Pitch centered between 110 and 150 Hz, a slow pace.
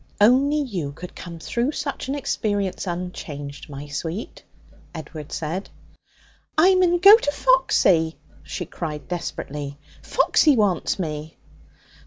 No: medium, 180 Hz; slow, 120 wpm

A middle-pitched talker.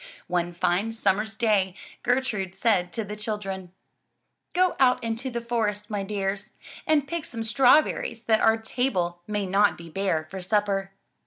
No: high, 210 Hz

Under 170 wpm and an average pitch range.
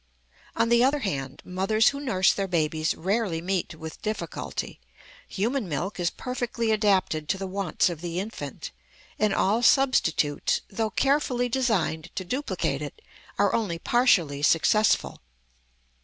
No: average, 140 wpm; wide, 6.0 semitones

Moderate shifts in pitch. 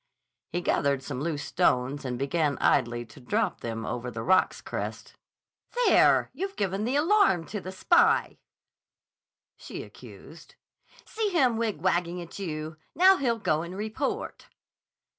No: wide, 8.2 semitones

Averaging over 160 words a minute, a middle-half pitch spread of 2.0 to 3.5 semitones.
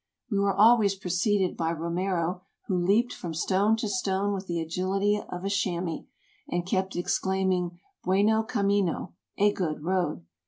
No: average, 155 wpm; narrow, 2.4 semitones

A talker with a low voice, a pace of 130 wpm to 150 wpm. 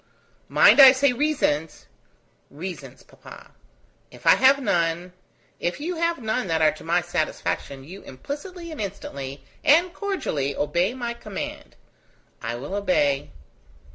No: medium, 185 Hz; average, 140 wpm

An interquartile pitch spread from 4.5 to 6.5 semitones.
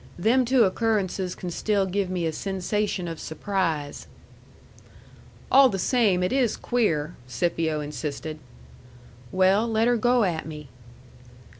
Yes: average, 5.3 semitones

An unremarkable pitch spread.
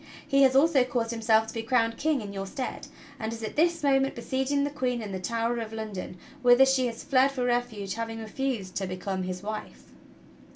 Yes: average, 3.5 semitones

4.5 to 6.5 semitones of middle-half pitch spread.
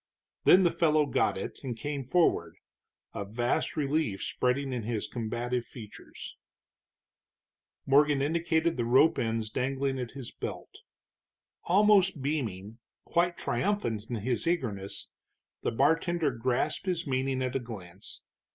Yes: average, 5.3 semitones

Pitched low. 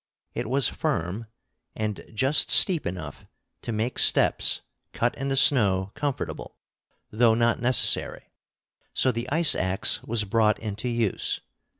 Yes: low, 115 Hz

